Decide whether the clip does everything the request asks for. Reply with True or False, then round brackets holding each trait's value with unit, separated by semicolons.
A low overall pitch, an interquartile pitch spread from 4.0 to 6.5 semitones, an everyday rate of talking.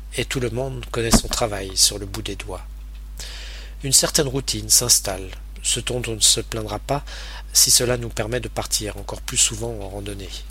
True (110 Hz; 4.7 semitones; 200 wpm)